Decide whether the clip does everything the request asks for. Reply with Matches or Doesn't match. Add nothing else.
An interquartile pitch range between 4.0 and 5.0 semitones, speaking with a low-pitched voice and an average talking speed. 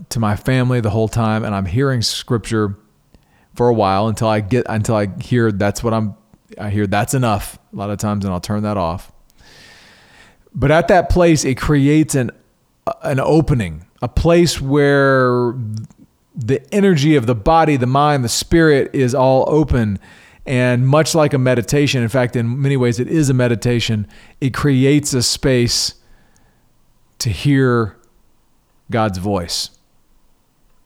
Matches